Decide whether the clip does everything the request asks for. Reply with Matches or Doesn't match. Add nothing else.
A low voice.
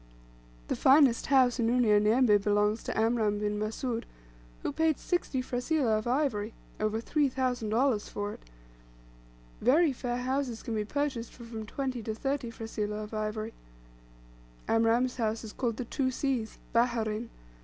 Doesn't match